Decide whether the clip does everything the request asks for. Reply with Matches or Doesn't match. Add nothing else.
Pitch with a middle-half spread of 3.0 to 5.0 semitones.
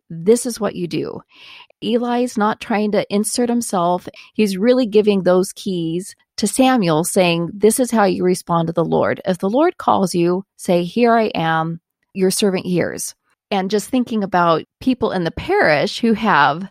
Matches